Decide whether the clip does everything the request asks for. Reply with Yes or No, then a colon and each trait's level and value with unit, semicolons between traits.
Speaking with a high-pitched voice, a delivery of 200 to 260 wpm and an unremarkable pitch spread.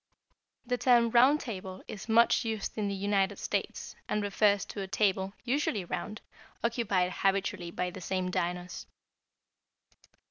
No: high, 200 Hz; average, 140 wpm; average, 3.3 semitones